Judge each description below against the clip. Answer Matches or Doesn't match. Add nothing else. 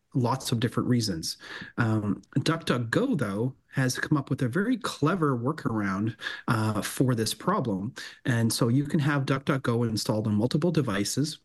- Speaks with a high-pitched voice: Doesn't match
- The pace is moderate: Matches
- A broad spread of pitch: Doesn't match